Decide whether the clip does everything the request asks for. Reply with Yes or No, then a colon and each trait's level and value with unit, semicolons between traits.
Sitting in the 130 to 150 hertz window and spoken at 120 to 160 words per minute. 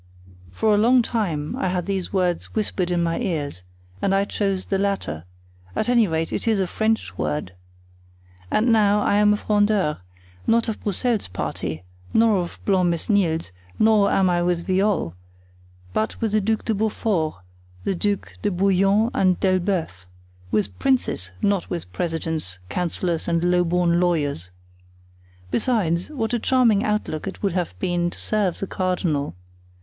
No: medium, 185 Hz; average, 155 wpm